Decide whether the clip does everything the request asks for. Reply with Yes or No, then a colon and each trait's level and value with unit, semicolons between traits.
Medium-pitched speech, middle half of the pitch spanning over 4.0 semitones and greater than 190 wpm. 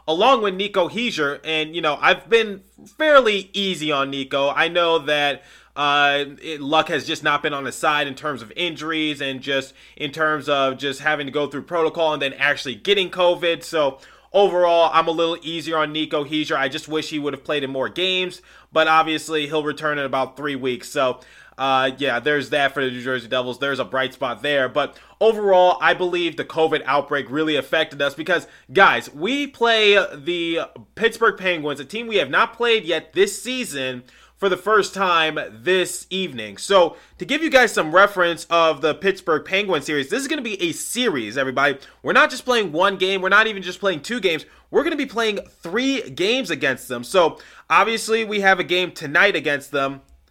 Yes: medium, 160 Hz; average, 5.2 semitones; fast, 205 wpm